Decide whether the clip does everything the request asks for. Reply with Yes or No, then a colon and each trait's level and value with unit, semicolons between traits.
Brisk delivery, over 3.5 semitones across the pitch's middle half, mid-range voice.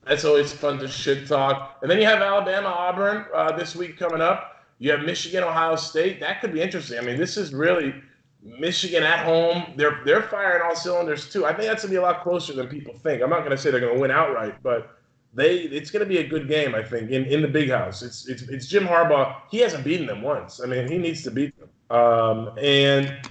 Yes: fast, 240 wpm; average, 4.5 semitones; medium, 155 Hz